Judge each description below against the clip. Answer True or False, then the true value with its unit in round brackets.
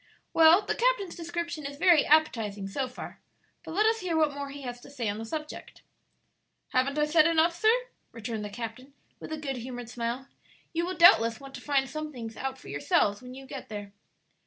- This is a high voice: True (280 Hz)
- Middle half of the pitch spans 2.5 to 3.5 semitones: False (5.3 semitones)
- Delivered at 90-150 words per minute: False (205 wpm)